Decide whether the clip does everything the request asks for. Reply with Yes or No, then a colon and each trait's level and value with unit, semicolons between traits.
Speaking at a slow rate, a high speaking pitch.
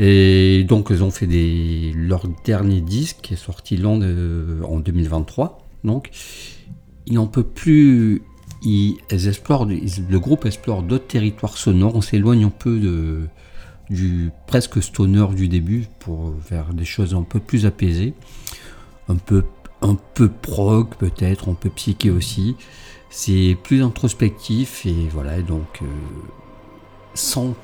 No: slow, 135 wpm; low, 100 Hz